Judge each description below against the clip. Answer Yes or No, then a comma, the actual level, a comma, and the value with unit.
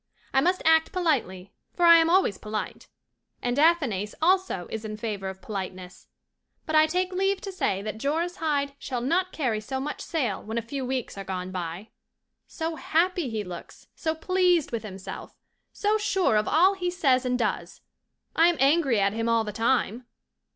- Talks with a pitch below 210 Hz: No, very high, 265 Hz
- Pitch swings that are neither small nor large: No, wide, 8.0 semitones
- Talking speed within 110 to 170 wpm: No, average, 185 wpm